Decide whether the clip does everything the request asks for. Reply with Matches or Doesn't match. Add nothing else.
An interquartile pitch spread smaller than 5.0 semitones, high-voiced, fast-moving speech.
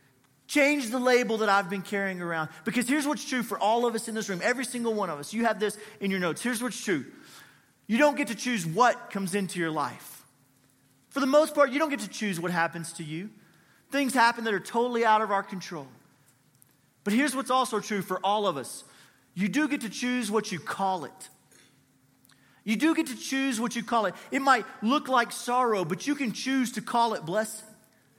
Doesn't match